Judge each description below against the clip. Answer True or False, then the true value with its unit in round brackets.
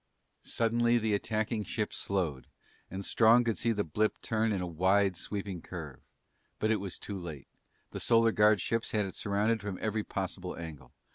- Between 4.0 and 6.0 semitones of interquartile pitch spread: False (3.2 semitones)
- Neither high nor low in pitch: False (105 Hz)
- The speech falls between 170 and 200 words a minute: True (180 wpm)